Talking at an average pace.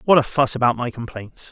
No: fast, 240 wpm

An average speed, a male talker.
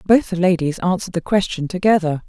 No: average, 185 wpm; female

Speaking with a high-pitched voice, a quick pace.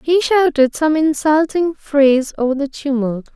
No: very high, 290 Hz; average, 145 wpm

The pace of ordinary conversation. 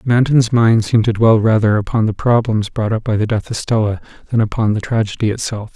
No: fast, 220 wpm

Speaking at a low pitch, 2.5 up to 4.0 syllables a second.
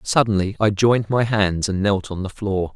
No: low, 100 Hz; 5.0 syllables/s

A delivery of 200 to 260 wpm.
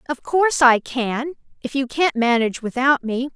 No: average, 180 wpm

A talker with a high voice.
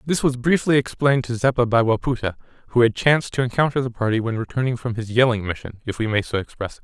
No: low, 120 Hz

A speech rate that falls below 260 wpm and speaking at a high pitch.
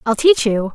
Yes: fast, 240 wpm; high, 245 Hz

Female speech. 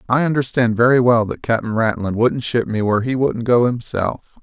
No: male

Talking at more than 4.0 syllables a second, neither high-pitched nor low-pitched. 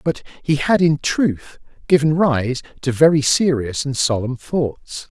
No: 3.9 syllables/s; medium, 145 Hz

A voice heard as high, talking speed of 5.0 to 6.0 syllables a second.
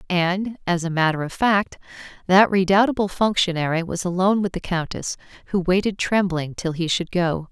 No: medium, 180 Hz; 5.2 syllables/s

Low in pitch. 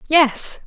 No: very high, 290 Hz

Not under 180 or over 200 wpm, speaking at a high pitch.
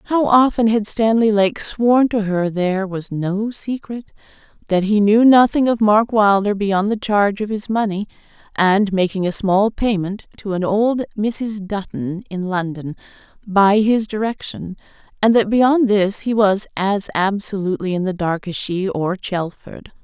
No: average, 165 wpm; high, 205 Hz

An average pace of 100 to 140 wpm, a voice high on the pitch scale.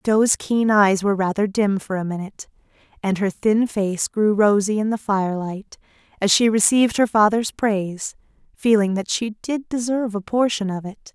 No: average, 180 wpm; high, 210 Hz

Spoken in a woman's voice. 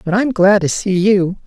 No: male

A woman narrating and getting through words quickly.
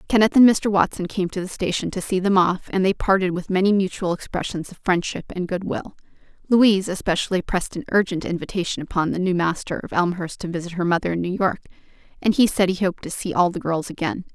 Yes: female; fast, 225 wpm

